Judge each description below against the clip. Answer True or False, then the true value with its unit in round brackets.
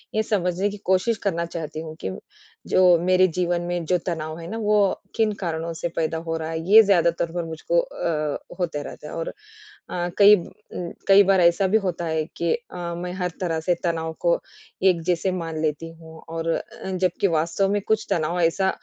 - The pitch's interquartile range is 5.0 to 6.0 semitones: False (2.6 semitones)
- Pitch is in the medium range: True (170 Hz)